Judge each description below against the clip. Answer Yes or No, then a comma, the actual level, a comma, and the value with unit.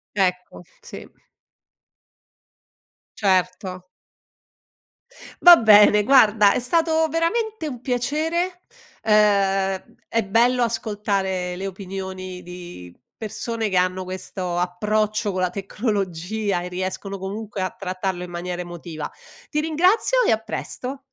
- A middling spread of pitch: Yes, average, 4.0 semitones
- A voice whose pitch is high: Yes, high, 200 Hz